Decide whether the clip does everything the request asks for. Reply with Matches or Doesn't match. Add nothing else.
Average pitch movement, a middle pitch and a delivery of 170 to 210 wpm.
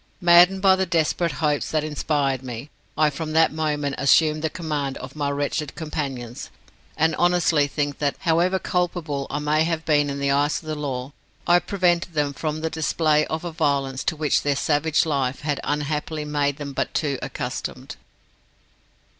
Doesn't match